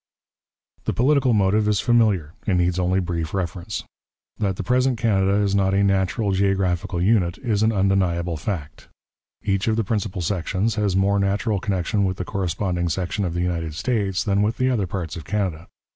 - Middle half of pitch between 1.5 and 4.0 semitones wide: Yes, average, 2.8 semitones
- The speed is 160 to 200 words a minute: Yes, average, 180 wpm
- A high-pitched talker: No, very low, 95 Hz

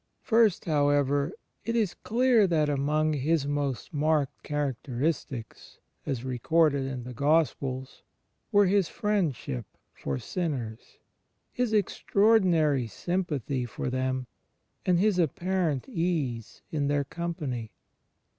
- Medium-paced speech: No, slow, 115 wpm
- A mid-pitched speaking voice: Yes, medium, 150 Hz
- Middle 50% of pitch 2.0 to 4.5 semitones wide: No, average, 5.2 semitones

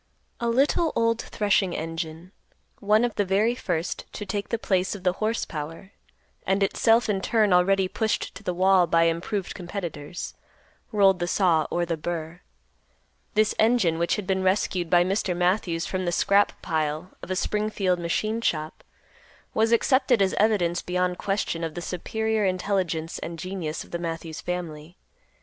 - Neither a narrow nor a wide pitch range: Yes, average, 3.5 semitones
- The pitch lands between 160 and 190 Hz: Yes, medium, 185 Hz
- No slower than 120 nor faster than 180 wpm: Yes, average, 165 wpm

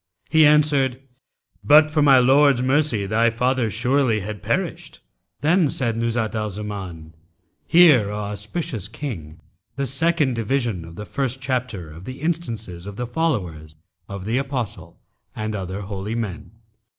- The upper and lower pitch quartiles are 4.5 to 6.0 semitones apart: Yes, average, 5.3 semitones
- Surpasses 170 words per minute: No, average, 145 wpm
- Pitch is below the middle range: Yes, low, 115 Hz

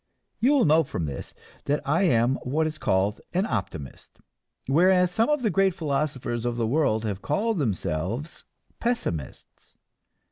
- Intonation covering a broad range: Yes, wide, 8.4 semitones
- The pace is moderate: Yes, average, 150 wpm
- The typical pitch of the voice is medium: Yes, medium, 145 Hz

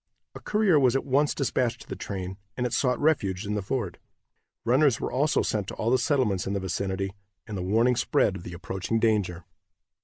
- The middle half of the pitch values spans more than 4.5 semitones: Yes, average, 5.2 semitones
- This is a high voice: No, low, 110 Hz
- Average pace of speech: No, fast, 210 wpm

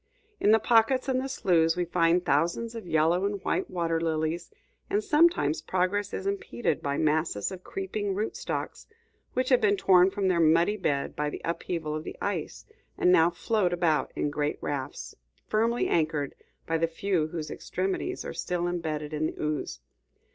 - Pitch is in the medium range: Yes, medium, 175 Hz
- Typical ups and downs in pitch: Yes, average, 4.2 semitones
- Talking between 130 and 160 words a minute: No, average, 175 wpm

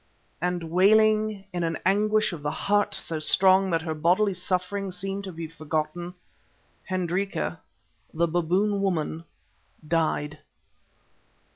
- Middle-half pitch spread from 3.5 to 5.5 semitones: No, average, 3.1 semitones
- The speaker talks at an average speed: No, slow, 120 wpm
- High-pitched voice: No, medium, 180 Hz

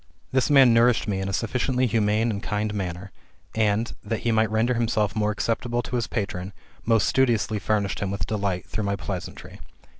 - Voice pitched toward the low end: Yes, low, 110 Hz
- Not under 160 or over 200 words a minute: Yes, average, 185 wpm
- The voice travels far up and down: No, narrow, 2.6 semitones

